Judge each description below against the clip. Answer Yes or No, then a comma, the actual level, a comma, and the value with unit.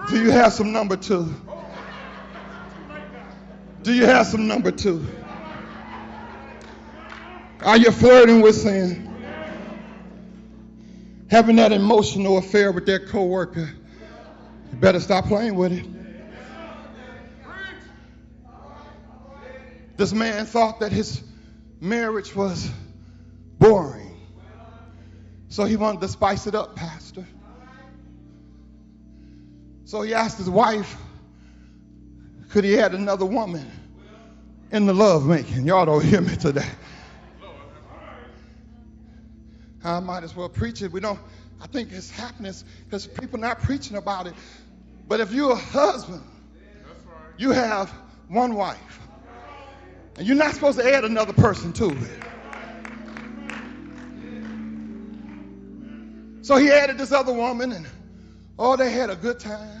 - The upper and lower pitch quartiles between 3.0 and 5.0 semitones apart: No, wide, 5.4 semitones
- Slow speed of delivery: Yes, slow, 115 wpm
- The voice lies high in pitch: Yes, high, 205 Hz